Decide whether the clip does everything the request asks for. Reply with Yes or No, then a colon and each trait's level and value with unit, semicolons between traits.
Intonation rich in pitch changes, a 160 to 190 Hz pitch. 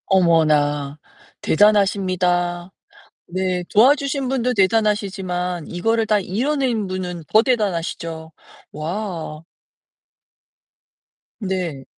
No: average, 3.9 semitones; medium, 185 Hz